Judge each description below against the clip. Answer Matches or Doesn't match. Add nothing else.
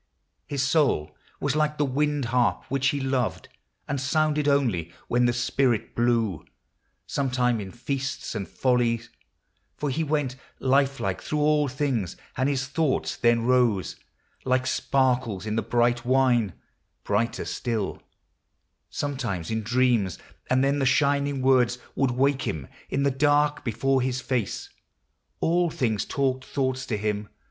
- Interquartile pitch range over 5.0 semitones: Doesn't match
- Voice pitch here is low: Matches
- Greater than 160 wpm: Doesn't match